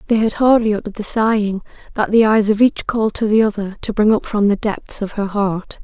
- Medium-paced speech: No, fast, 245 wpm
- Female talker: Yes, female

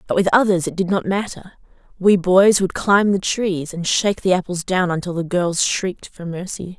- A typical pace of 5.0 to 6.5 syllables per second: Yes, 5.1 syllables/s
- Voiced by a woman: Yes, female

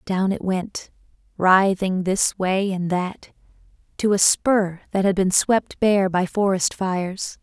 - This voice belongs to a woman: Yes, female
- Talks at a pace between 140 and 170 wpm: Yes, average, 155 wpm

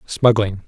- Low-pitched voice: Yes, low, 105 Hz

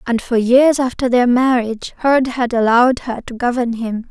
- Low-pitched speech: No, high, 245 Hz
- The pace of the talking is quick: No, average, 190 wpm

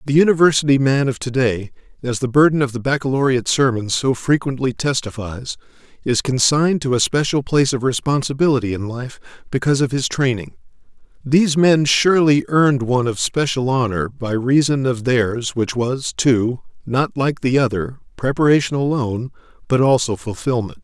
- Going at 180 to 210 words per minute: No, average, 155 wpm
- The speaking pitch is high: No, low, 130 Hz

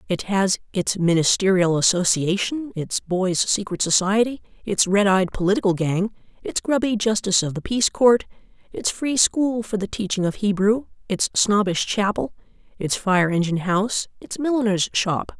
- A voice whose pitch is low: No, high, 200 Hz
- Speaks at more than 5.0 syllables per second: No, 4.8 syllables/s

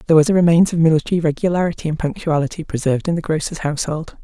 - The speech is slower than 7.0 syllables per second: No, 7.7 syllables/s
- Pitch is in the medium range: Yes, medium, 160 Hz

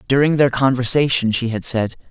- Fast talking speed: No, average, 170 wpm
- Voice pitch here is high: No, low, 125 Hz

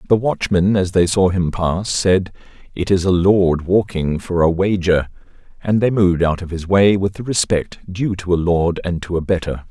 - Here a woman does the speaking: No, male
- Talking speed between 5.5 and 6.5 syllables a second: No, 4.7 syllables/s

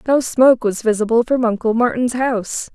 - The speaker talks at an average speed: Yes, average, 175 wpm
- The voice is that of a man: No, female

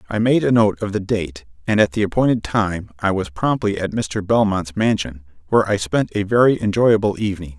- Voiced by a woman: No, male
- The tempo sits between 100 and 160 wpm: No, fast, 205 wpm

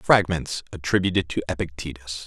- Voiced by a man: Yes, male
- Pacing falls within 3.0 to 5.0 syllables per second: No, 5.3 syllables/s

